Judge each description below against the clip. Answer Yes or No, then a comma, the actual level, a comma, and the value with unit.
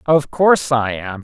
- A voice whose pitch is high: No, low, 130 Hz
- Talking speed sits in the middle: Yes, average, 195 wpm